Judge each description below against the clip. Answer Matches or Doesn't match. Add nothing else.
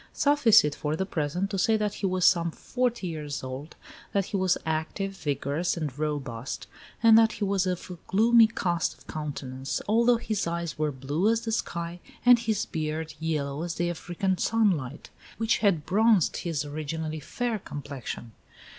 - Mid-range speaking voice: Matches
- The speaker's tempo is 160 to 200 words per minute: Matches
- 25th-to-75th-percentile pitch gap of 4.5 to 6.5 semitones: Matches